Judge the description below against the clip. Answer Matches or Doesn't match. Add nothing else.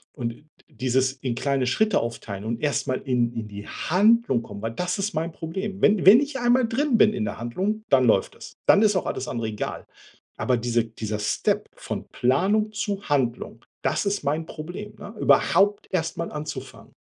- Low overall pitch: Doesn't match